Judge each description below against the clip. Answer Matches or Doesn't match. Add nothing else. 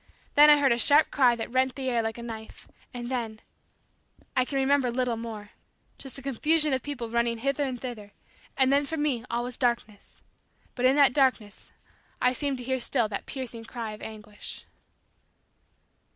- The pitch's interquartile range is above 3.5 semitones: Doesn't match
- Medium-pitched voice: Doesn't match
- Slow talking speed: Doesn't match